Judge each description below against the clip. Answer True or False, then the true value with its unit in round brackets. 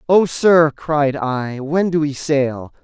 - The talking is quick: False (170 wpm)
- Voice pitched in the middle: True (150 Hz)